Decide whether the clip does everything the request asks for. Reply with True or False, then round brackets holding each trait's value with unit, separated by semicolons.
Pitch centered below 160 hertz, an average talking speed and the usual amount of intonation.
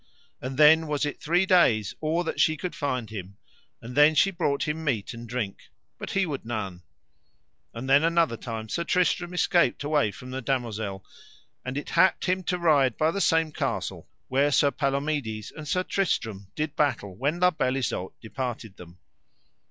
False (140 Hz; 180 wpm; 5.8 semitones)